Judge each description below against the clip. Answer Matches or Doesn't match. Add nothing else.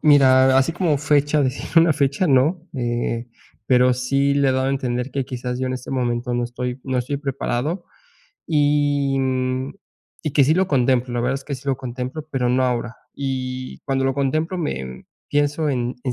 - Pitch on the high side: Doesn't match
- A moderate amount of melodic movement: Doesn't match